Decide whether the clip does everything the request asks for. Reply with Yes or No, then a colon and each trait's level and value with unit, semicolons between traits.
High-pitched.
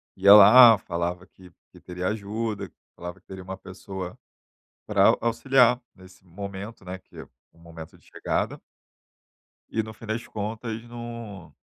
No: low, 100 Hz